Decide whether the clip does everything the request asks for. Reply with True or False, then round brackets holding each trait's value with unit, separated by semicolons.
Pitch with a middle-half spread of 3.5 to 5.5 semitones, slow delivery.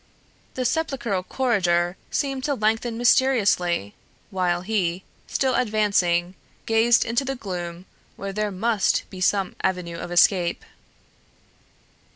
True (5.0 semitones; 115 wpm)